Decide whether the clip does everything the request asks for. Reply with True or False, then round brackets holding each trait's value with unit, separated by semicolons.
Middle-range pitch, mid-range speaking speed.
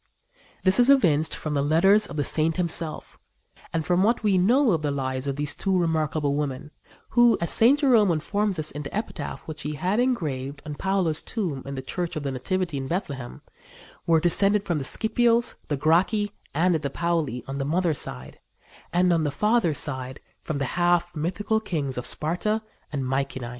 True (165 Hz; 190 wpm)